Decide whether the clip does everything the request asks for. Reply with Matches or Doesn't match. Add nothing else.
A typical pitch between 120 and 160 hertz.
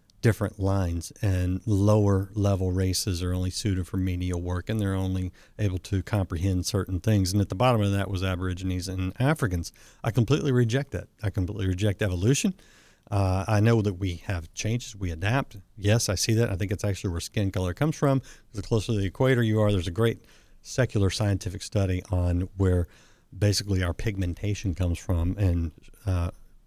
Doesn't match